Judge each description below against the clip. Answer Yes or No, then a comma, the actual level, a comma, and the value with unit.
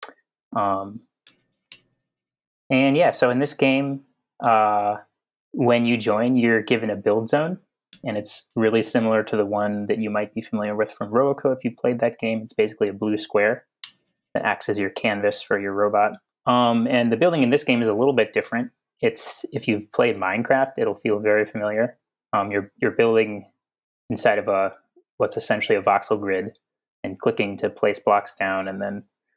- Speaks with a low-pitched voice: Yes, low, 110 Hz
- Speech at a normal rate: Yes, average, 185 wpm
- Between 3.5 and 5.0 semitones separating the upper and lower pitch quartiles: Yes, average, 3.9 semitones